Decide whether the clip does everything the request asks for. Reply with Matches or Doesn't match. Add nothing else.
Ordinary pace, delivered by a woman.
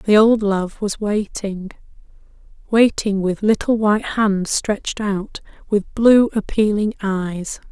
Doesn't match